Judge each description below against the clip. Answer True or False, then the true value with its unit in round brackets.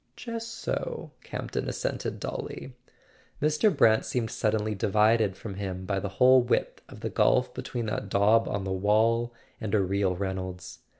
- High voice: False (105 Hz)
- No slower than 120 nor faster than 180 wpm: True (160 wpm)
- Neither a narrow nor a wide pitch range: True (3.4 semitones)